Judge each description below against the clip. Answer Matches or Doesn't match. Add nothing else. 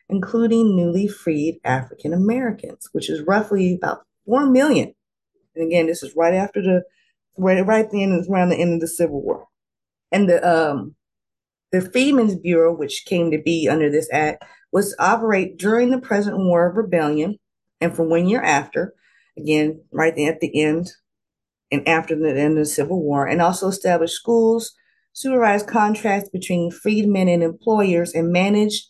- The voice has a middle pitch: Matches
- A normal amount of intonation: Matches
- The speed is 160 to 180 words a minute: Matches